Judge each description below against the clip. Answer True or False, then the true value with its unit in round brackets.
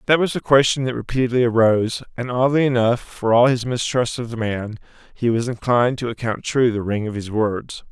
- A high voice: False (120 Hz)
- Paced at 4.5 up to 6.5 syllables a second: True (5.6 syllables/s)